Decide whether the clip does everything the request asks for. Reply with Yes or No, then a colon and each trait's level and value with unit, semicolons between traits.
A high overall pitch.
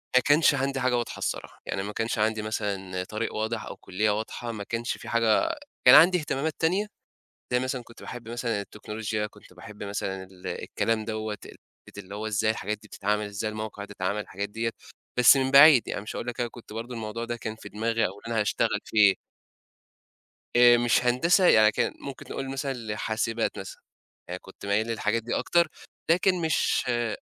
No: low, 115 Hz